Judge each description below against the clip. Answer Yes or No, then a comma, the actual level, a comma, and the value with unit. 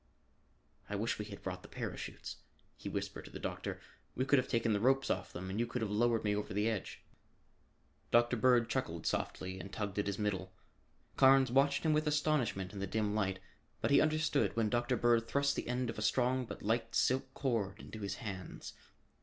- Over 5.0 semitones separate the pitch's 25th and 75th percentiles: No, average, 4.0 semitones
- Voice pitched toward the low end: Yes, low, 115 Hz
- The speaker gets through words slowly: No, fast, 205 wpm